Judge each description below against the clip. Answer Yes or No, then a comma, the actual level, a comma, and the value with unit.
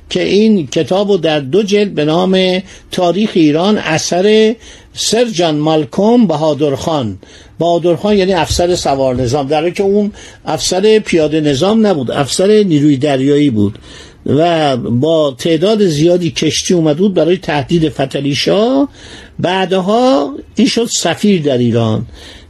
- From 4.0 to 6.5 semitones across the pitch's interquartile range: Yes, average, 5.2 semitones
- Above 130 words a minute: No, average, 125 wpm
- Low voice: No, medium, 170 Hz